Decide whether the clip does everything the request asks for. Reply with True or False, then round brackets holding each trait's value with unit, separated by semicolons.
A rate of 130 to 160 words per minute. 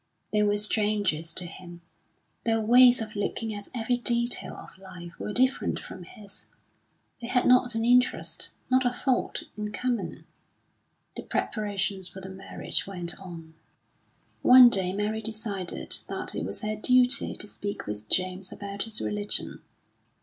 True (150 wpm)